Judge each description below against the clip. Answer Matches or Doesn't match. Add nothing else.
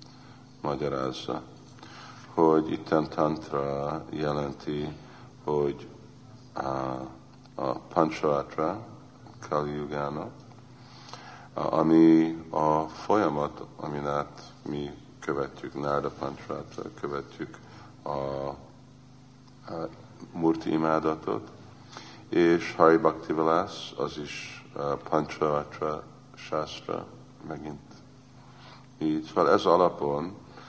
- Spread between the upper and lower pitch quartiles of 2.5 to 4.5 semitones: Matches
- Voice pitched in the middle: Doesn't match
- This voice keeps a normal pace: Doesn't match